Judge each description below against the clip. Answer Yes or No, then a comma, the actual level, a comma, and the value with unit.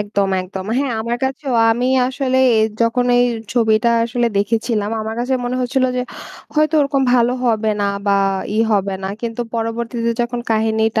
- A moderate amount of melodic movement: No, narrow, 2.3 semitones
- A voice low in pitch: No, high, 235 Hz